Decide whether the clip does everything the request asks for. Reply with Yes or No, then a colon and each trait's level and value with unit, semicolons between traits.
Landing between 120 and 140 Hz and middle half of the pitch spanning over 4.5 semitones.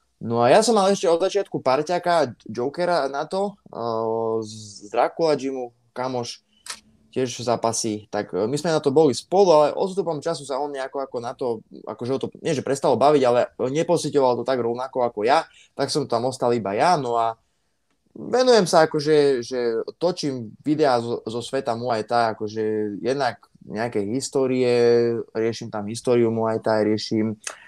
Yes: low, 125 Hz; average, 4.9 semitones